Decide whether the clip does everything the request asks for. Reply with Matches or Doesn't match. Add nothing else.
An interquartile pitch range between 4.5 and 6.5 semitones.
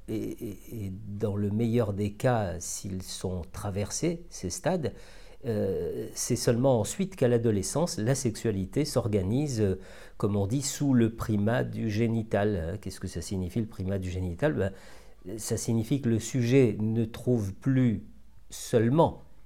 Doesn't match